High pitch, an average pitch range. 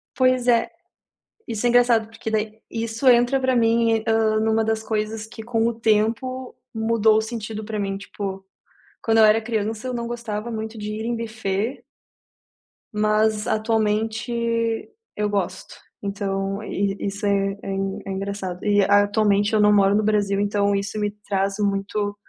No: high, 215 Hz; narrow, 1.9 semitones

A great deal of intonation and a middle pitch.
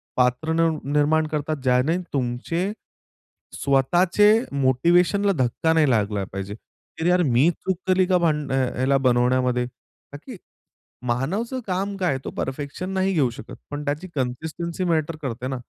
Yes: wide, 5.7 semitones; medium, 150 Hz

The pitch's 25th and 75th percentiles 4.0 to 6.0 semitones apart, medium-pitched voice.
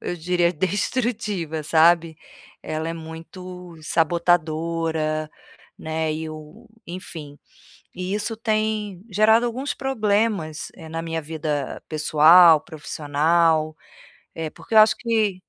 Yes: average, 4.4 semitones; medium, 165 Hz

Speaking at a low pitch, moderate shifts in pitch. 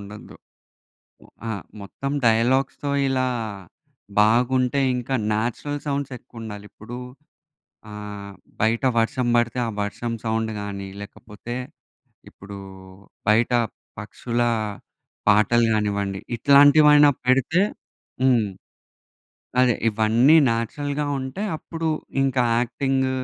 Yes: low, 120 Hz; average, 3.8 semitones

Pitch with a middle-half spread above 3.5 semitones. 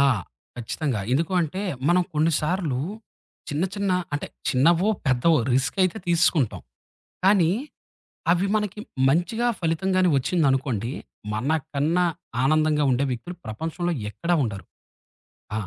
Yes: average, 4.7 semitones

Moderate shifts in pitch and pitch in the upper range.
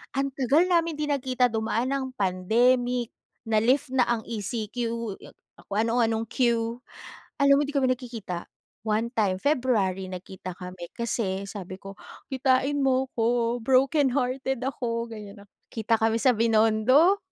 Yes: average, 3.5 semitones; high, 235 Hz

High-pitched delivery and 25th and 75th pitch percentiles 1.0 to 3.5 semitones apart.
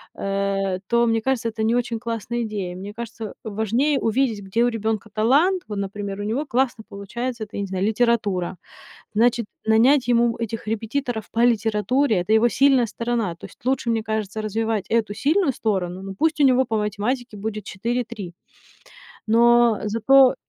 Yes: high, 225 Hz; average, 2.7 semitones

